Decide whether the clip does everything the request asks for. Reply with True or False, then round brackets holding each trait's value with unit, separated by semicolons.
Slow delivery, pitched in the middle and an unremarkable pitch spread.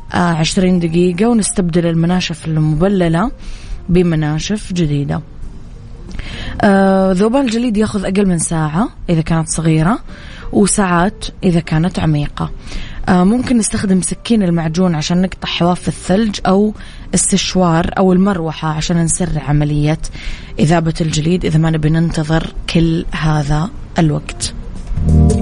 True (110 wpm; 170 Hz; 3.6 semitones)